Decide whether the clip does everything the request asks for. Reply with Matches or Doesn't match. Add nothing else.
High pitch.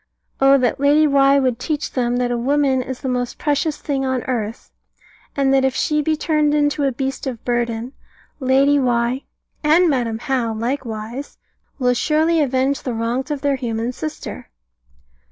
Matches